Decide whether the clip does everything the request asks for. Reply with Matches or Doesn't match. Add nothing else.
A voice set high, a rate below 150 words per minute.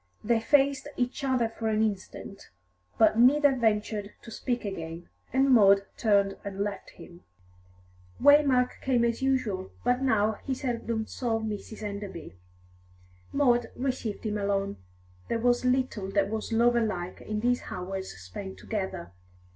Matches